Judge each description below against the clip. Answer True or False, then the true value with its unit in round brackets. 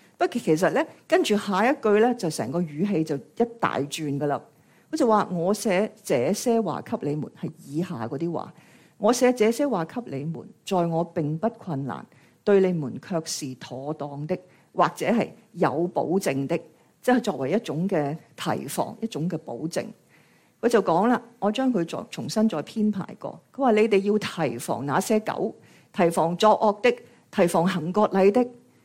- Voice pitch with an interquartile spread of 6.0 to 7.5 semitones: False (5.5 semitones)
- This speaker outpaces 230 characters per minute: True (250 characters per minute)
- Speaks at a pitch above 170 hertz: True (185 Hz)